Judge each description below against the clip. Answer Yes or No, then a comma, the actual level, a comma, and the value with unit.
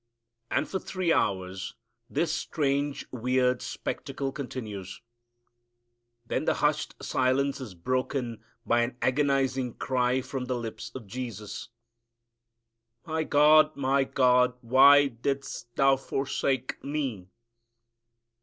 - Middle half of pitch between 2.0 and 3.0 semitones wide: Yes, average, 2.7 semitones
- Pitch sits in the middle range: No, low, 130 Hz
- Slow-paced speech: Yes, slow, 105 wpm